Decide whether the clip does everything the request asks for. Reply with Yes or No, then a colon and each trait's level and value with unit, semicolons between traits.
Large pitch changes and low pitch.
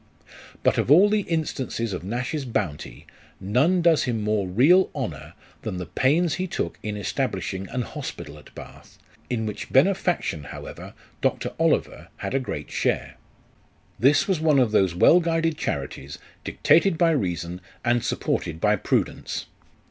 Yes: wide, 9.0 semitones; low, 125 Hz